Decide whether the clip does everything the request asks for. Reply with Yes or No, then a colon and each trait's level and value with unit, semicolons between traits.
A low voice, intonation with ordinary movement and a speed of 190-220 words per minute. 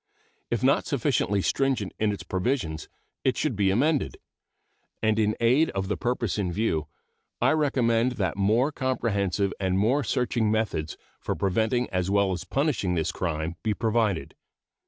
No: low, 105 Hz; average, 4.4 semitones; average, 155 wpm